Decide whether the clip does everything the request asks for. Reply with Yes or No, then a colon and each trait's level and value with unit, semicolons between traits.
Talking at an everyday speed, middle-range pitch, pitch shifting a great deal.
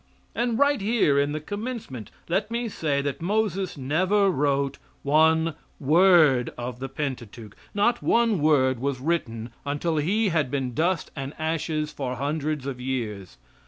Yes: average, 150 wpm; medium, 150 Hz; wide, 5.9 semitones